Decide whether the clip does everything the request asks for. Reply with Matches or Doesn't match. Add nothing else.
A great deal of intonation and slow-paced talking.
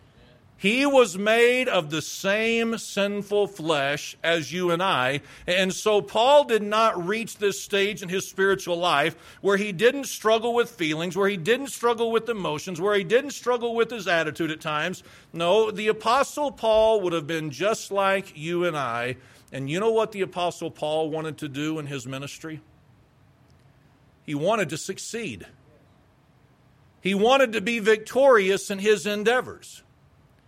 Doesn't match